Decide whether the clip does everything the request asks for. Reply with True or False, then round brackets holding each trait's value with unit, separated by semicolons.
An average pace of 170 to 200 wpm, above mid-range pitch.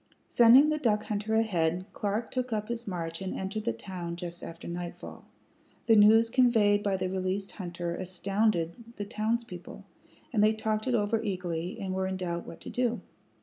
True (180 wpm; 205 Hz)